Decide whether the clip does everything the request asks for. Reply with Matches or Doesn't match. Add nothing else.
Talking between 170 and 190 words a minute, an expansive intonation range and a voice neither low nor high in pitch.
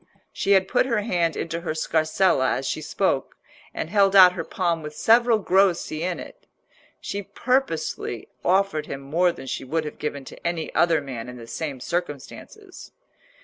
Doesn't match